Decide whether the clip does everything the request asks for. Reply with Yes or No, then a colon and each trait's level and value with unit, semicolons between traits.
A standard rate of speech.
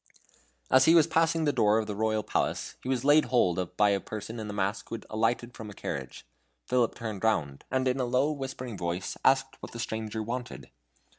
No: fast, 220 wpm